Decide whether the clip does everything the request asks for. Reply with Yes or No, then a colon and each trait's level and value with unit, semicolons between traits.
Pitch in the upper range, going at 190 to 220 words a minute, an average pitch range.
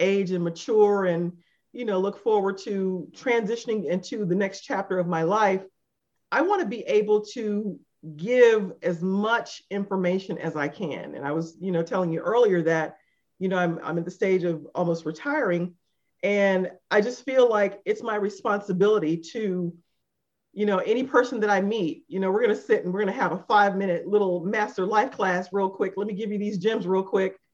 Yes: high, 195 Hz; average, 200 wpm; average, 3.0 semitones